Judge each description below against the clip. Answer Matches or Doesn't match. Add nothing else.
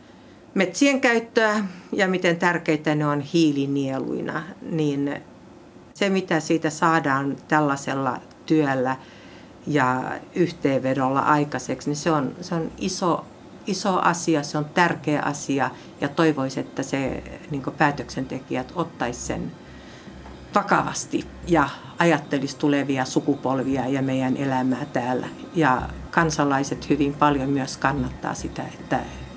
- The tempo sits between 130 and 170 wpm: Doesn't match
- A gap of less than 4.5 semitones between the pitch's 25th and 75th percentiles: Matches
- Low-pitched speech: Doesn't match